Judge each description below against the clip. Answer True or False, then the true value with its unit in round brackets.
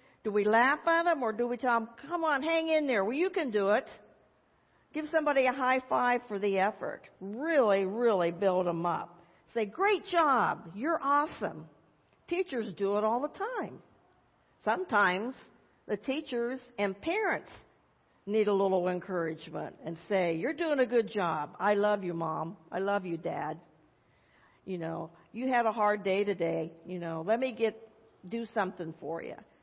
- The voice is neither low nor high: False (215 Hz)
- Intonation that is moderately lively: False (5.9 semitones)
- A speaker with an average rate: True (170 wpm)